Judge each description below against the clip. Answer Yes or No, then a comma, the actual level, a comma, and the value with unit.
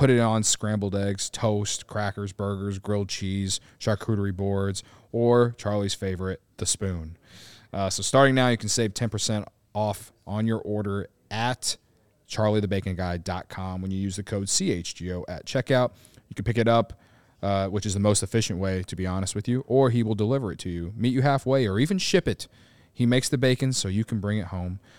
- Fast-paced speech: No, average, 190 wpm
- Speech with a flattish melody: No, average, 3.3 semitones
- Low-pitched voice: Yes, low, 105 Hz